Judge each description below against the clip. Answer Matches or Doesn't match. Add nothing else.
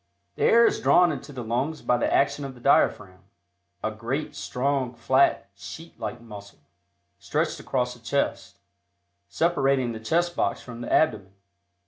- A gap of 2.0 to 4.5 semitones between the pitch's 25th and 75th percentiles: Matches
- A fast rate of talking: Doesn't match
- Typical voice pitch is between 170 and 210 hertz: Doesn't match